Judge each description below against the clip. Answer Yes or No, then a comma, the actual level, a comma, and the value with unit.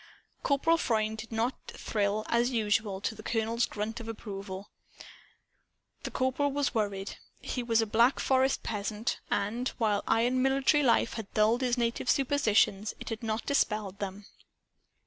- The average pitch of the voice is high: Yes, high, 225 Hz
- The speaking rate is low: No, average, 150 wpm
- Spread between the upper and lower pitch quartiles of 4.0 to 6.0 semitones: No, average, 3.1 semitones